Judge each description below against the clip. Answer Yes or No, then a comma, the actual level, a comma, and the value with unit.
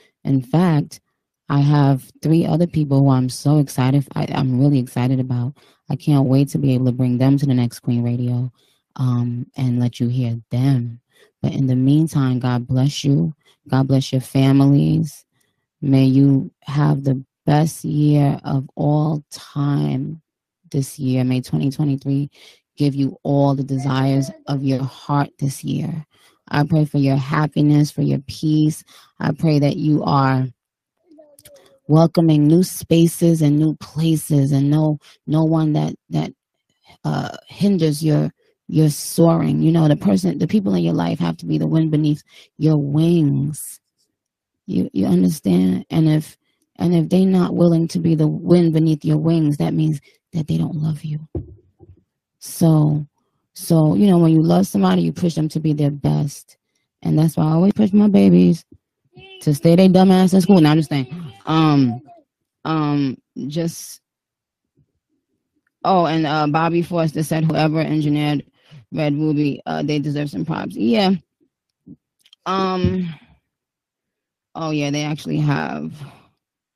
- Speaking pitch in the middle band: Yes, medium, 150 Hz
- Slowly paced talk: No, average, 155 wpm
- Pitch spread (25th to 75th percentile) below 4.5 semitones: Yes, average, 3.0 semitones